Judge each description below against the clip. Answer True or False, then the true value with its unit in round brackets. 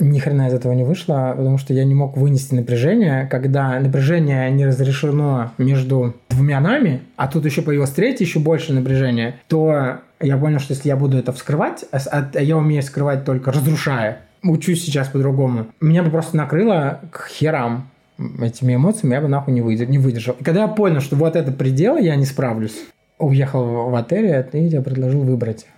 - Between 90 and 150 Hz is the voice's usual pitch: True (140 Hz)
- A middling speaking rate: False (180 wpm)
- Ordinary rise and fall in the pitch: True (3.2 semitones)